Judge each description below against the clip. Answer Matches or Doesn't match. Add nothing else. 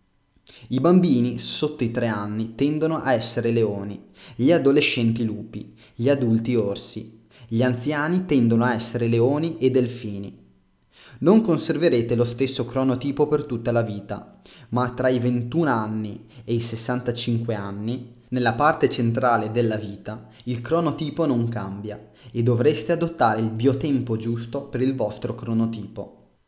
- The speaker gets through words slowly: Doesn't match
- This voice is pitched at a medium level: Doesn't match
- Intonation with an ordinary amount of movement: Matches